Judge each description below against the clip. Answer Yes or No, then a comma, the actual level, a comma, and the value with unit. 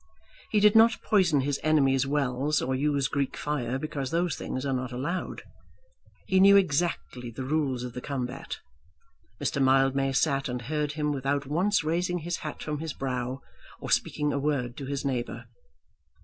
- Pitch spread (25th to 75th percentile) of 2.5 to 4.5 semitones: Yes, average, 2.9 semitones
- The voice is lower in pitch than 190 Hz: Yes, medium, 140 Hz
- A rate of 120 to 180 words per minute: Yes, average, 170 wpm